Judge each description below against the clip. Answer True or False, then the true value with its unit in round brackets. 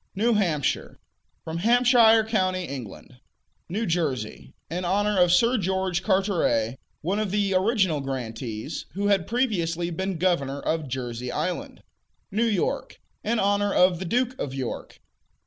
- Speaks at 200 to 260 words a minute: False (140 wpm)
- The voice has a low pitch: False (185 Hz)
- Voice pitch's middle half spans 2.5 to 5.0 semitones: False (5.5 semitones)